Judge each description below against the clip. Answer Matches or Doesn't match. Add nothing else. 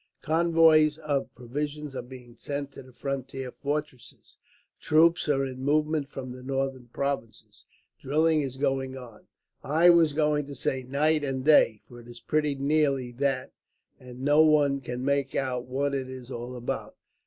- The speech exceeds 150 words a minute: Matches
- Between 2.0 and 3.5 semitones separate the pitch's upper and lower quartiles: Matches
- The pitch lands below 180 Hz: Matches